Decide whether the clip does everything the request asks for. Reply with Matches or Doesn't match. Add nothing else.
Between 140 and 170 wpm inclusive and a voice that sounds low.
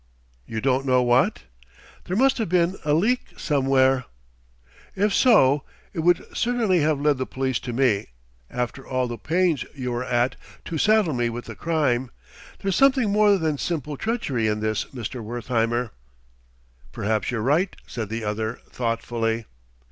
Matches